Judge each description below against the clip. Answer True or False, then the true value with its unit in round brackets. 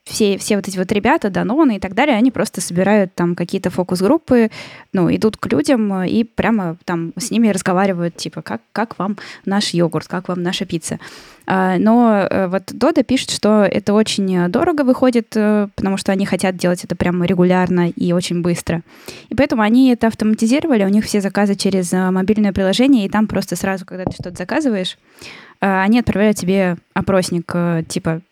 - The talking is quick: True (175 wpm)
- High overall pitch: True (195 Hz)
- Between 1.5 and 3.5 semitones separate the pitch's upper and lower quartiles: True (3.2 semitones)